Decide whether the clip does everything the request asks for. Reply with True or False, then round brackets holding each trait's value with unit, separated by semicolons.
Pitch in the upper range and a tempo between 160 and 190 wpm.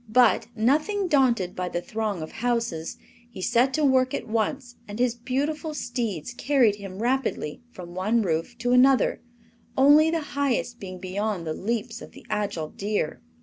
True (235 Hz; 165 wpm)